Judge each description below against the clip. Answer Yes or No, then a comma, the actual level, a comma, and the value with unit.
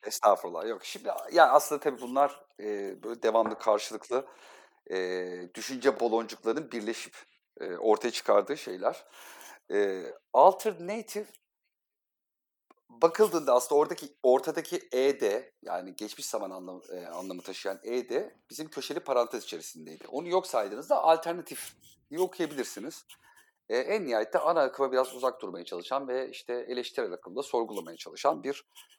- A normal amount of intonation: No, wide, 6.7 semitones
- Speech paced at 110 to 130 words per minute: Yes, average, 125 wpm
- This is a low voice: Yes, low, 130 Hz